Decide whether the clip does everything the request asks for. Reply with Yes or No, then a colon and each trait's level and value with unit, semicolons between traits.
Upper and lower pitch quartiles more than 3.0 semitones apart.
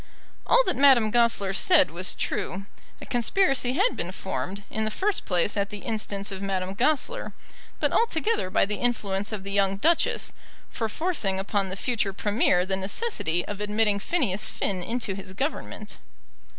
Yes: average, 4.7 semitones